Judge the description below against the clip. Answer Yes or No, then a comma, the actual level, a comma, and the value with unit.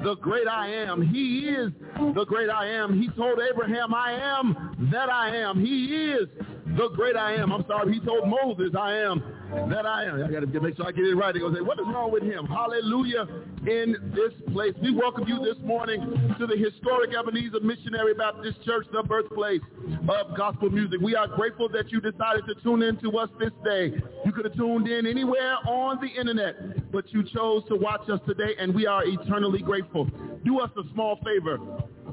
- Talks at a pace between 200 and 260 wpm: Yes, fast, 205 wpm